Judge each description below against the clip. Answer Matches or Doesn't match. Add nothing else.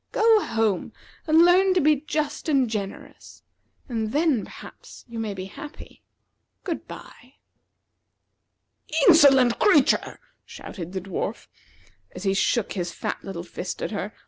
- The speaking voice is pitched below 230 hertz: Doesn't match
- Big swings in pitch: Matches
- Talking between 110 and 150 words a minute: Matches